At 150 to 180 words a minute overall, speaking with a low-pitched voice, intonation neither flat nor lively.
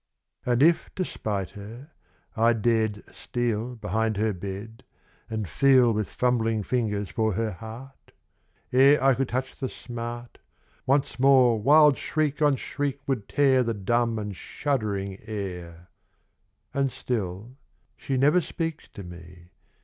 No: average, 140 wpm; low, 115 Hz; average, 4.4 semitones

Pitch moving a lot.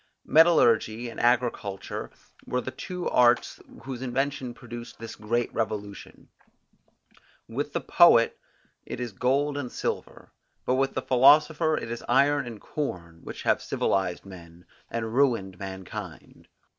No: average, 4.0 semitones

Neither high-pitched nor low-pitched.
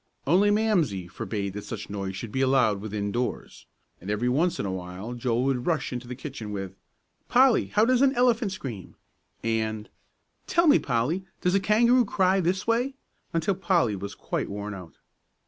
No: low, 125 Hz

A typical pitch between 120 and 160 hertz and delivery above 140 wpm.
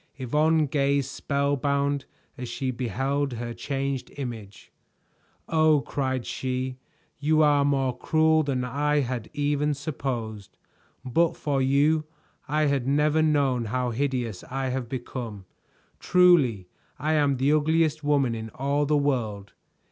No: medium, 140 Hz; slow, 135 wpm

